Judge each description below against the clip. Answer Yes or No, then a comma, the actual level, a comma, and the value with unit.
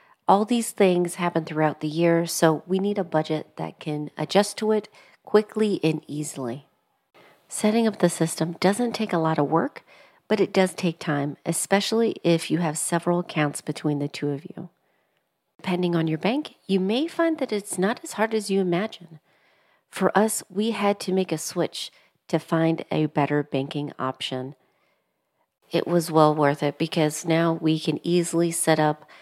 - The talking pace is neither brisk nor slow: Yes, average, 180 wpm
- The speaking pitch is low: No, medium, 170 Hz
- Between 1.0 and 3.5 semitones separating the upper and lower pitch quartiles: No, average, 4.2 semitones